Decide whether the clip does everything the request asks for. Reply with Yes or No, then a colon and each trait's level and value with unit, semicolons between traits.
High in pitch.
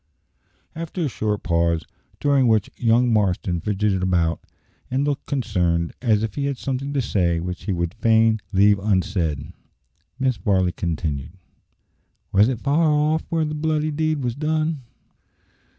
No: low, 110 Hz